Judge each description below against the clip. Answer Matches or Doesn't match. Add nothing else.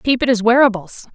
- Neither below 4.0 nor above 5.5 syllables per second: Doesn't match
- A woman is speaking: Matches